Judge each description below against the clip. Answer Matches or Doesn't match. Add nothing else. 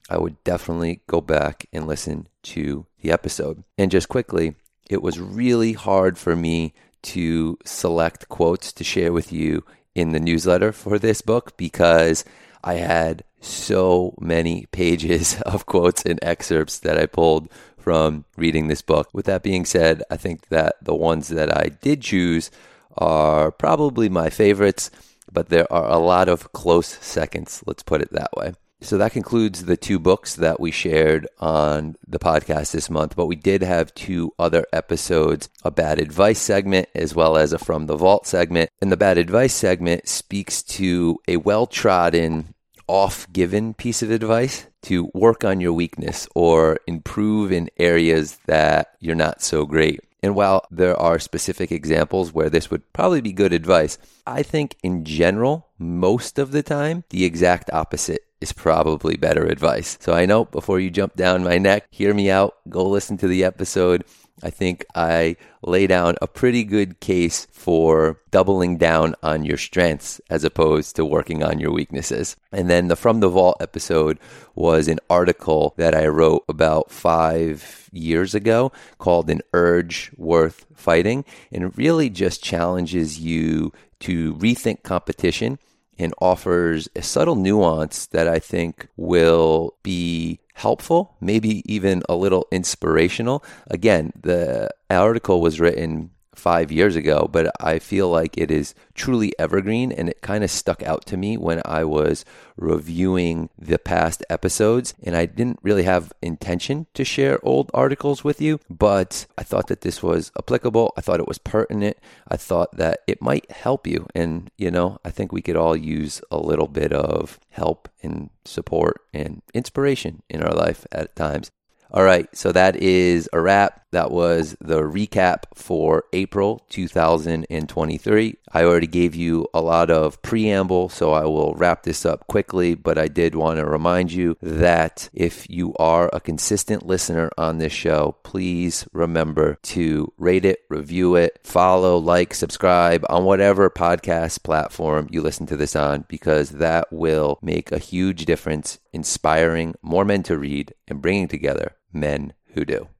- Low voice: Matches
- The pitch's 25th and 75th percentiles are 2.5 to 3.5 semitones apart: Matches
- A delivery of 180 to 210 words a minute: Doesn't match